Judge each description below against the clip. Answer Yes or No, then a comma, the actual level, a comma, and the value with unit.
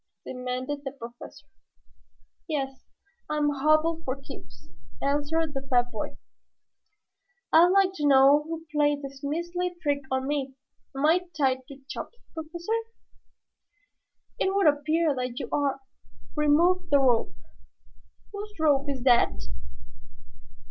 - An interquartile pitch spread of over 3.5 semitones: No, average, 3.2 semitones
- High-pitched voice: Yes, very high, 290 Hz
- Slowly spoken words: Yes, slow, 120 wpm